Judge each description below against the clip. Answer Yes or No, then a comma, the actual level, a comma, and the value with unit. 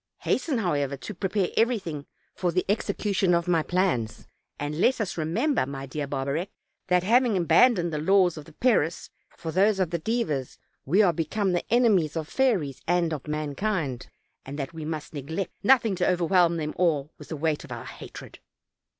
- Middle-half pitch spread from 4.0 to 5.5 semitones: Yes, average, 4.6 semitones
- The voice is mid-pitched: Yes, medium, 170 Hz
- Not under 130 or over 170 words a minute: No, average, 180 wpm